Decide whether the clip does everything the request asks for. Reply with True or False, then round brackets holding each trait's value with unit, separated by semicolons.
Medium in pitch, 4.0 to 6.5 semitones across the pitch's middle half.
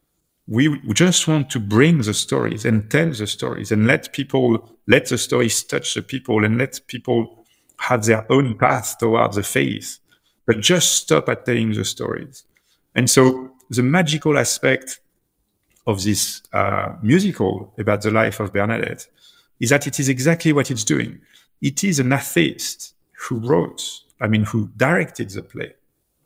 False (125 Hz; 4.7 semitones)